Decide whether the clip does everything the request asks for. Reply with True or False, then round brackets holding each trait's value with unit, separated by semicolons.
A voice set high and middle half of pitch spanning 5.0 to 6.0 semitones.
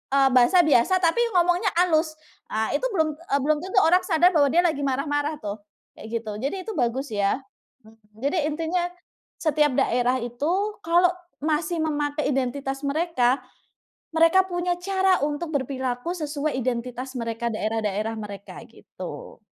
True (290 Hz; 5.5 semitones)